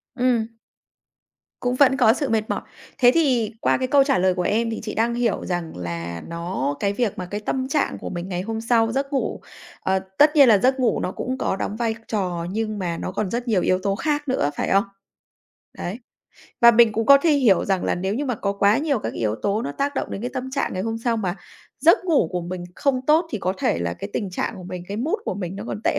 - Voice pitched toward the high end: Yes, high, 220 Hz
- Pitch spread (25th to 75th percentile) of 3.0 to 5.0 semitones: No, wide, 5.6 semitones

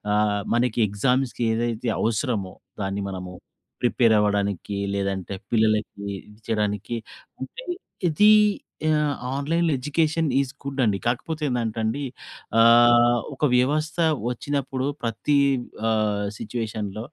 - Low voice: Yes, low, 115 Hz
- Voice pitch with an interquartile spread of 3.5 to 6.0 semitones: Yes, average, 4.6 semitones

